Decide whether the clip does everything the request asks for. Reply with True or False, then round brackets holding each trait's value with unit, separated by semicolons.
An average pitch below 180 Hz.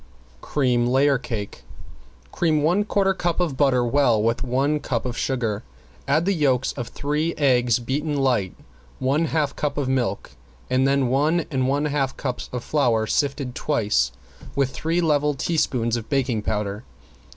True (135 Hz)